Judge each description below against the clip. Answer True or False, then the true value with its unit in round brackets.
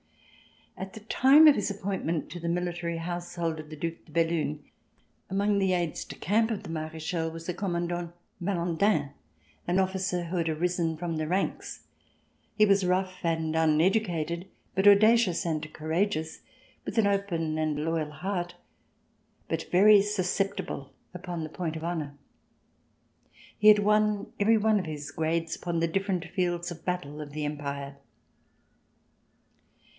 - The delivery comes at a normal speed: True (150 wpm)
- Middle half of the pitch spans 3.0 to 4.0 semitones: True (3.3 semitones)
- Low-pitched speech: False (175 Hz)